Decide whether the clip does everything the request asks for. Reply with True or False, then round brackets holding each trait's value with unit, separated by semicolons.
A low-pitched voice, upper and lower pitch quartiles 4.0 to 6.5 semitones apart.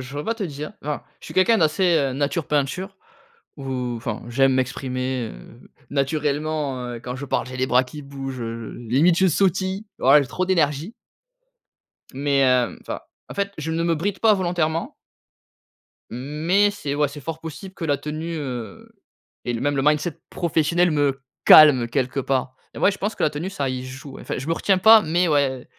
False (145 Hz; 4.3 semitones)